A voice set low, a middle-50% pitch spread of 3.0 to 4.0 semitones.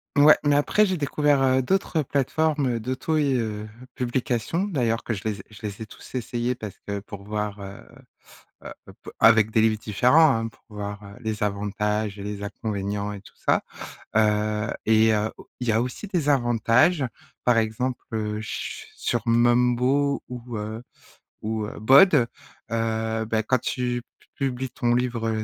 Yes: low, 115 Hz; average, 3.4 semitones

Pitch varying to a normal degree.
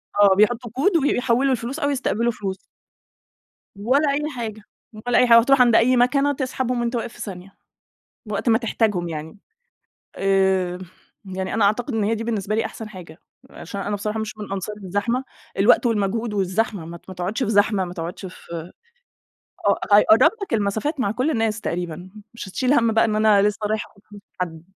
Yes: average, 3.7 semitones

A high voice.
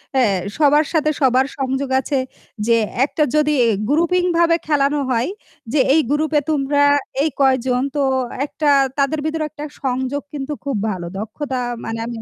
Yes: very high, 285 Hz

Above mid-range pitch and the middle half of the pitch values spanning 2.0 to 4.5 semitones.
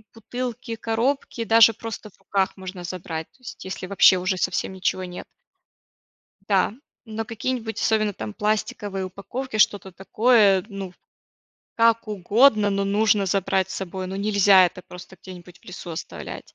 Yes: high, 200 Hz; average, 3.0 semitones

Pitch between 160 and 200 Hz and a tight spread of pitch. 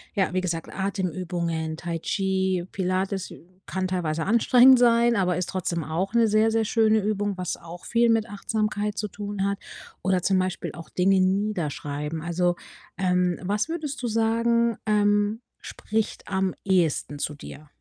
No: high, 190 Hz; average, 3.3 semitones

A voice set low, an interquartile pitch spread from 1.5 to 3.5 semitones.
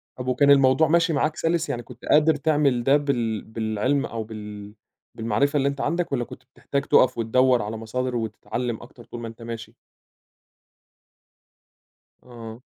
No: low, 125 Hz; average, 4.0 semitones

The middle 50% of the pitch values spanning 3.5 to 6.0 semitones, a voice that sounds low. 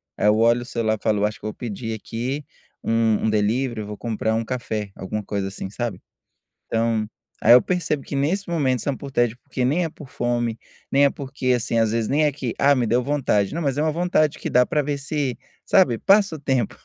Yes: average, 4.2 semitones; low, 120 Hz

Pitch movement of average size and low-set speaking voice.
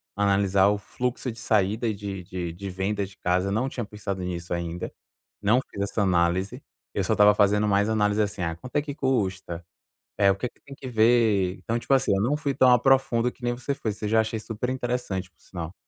Yes: average, 4.0 semitones; low, 105 Hz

